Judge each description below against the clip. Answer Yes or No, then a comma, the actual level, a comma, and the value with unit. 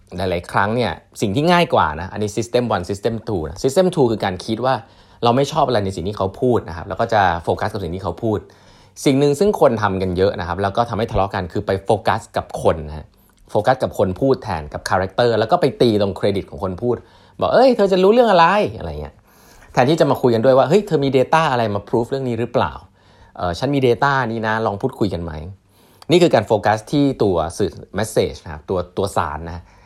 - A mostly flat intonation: No, wide, 5.6 semitones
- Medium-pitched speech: No, low, 110 Hz